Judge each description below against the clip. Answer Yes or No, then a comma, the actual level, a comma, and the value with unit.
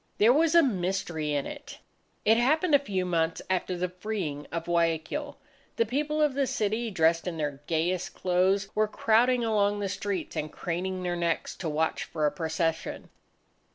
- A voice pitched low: No, medium, 185 Hz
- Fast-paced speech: No, average, 175 wpm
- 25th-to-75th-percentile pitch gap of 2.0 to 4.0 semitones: No, average, 5.2 semitones